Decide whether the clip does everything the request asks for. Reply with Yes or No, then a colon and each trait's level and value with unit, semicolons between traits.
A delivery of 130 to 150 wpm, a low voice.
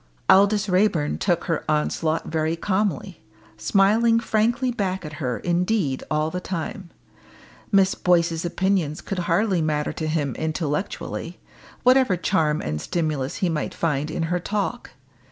No: slow, 135 wpm; medium, 175 Hz